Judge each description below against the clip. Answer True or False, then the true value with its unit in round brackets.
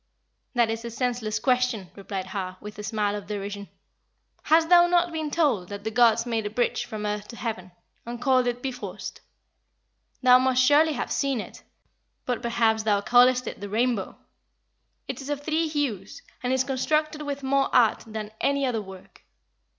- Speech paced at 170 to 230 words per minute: True (180 wpm)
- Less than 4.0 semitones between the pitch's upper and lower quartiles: False (4.4 semitones)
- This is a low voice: False (240 Hz)